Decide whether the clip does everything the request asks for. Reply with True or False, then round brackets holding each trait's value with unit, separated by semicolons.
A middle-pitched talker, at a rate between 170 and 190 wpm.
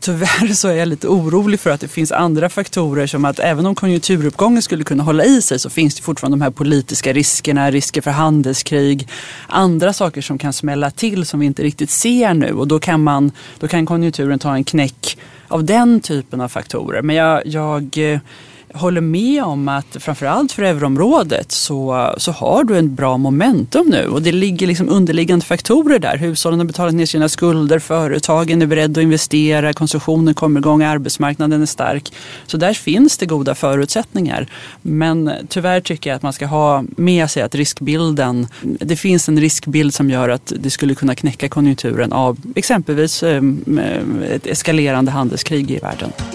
True (155 Hz; 180 wpm)